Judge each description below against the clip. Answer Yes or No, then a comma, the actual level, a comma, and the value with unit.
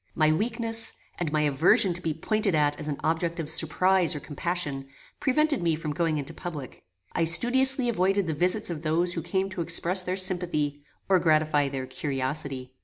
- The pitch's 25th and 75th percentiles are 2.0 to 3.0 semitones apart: No, average, 3.7 semitones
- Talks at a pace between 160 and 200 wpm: Yes, average, 180 wpm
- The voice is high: No, medium, 165 Hz